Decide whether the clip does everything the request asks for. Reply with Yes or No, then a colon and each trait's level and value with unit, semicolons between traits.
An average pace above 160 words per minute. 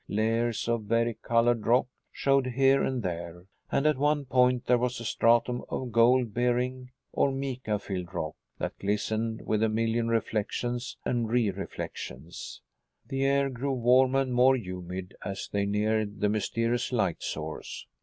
No: average, 155 wpm